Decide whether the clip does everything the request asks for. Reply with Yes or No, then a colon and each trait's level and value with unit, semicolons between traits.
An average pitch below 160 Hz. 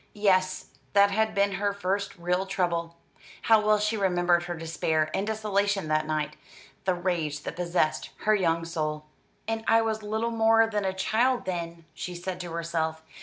No: medium, 185 Hz